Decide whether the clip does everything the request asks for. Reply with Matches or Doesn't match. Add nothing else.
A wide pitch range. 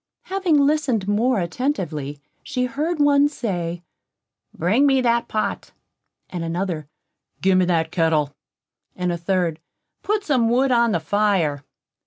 Matches